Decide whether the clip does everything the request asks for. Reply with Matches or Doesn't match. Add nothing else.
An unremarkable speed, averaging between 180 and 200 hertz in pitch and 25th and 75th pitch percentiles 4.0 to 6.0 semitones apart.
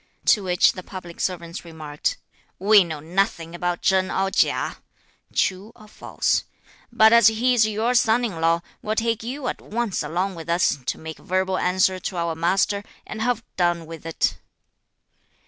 Matches